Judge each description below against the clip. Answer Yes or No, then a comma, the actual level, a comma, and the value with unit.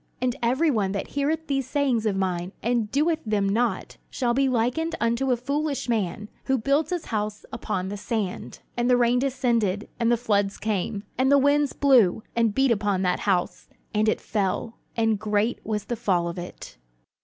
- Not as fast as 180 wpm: No, average, 190 wpm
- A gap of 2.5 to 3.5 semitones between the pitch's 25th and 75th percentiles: No, average, 4.5 semitones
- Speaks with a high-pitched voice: Yes, high, 230 Hz